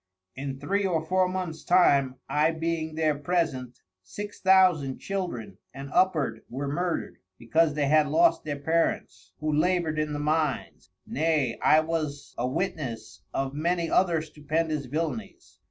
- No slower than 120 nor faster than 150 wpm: Yes, average, 145 wpm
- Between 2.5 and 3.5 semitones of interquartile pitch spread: Yes, average, 3.2 semitones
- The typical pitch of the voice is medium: Yes, medium, 155 Hz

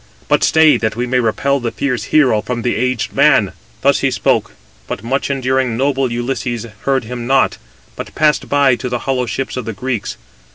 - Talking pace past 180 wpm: Yes, average, 195 wpm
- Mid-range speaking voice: No, low, 125 Hz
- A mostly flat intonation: Yes, narrow, 2.2 semitones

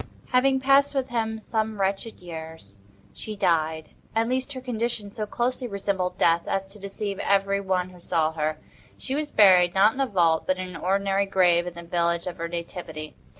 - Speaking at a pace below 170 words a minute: No, average, 185 wpm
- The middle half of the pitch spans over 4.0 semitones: Yes, average, 4.4 semitones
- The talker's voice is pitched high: Yes, high, 195 Hz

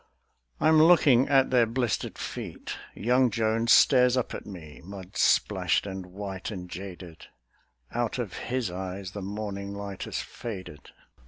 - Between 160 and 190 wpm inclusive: No, average, 150 wpm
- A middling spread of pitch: Yes, average, 4.4 semitones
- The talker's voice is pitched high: No, low, 100 Hz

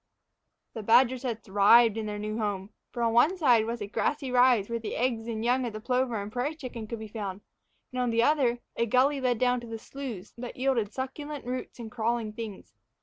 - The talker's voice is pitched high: Yes, high, 235 Hz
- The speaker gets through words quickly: Yes, fast, 220 wpm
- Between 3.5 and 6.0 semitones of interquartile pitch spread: No, average, 2.7 semitones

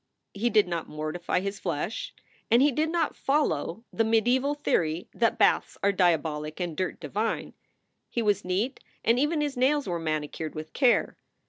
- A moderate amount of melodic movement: No, wide, 7.5 semitones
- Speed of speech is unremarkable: Yes, average, 170 wpm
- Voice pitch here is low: No, high, 200 Hz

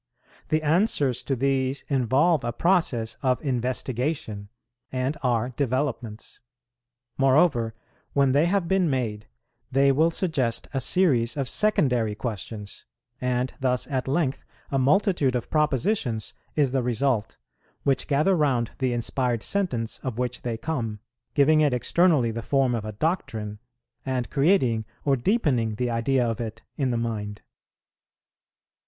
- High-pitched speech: No, low, 130 Hz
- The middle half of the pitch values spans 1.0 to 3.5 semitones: No, average, 3.9 semitones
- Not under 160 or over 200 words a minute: No, slow, 135 wpm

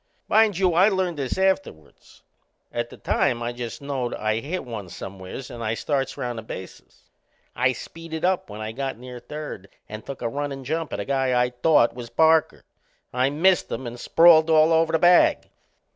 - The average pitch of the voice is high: No, low, 135 Hz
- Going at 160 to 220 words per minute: Yes, average, 190 wpm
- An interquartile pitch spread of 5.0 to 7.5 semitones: Yes, average, 5.3 semitones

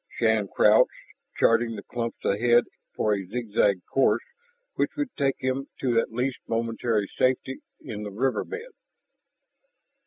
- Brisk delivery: No, slow, 135 wpm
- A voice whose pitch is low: Yes, low, 115 Hz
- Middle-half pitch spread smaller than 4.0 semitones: Yes, average, 3.4 semitones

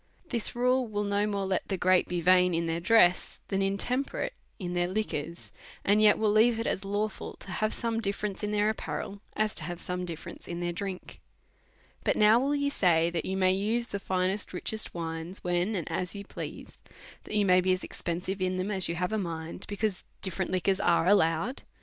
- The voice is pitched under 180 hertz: No, high, 190 Hz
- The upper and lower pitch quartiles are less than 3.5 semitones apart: Yes, average, 3.1 semitones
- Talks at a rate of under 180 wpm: No, average, 185 wpm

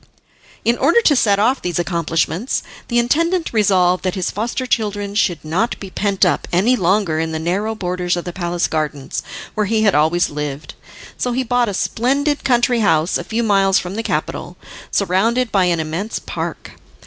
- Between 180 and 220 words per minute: Yes, average, 185 wpm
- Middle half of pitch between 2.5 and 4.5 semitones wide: No, average, 5.1 semitones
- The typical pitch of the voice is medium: No, high, 200 Hz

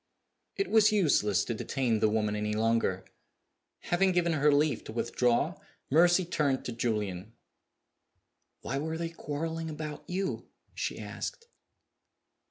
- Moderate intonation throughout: No, wide, 6.9 semitones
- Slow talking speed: Yes, slow, 130 wpm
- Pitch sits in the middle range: Yes, medium, 145 Hz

